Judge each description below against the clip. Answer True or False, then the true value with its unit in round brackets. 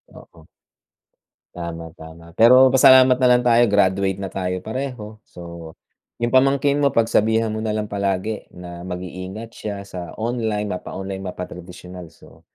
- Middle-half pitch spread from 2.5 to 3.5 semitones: False (4.3 semitones)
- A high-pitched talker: False (100 Hz)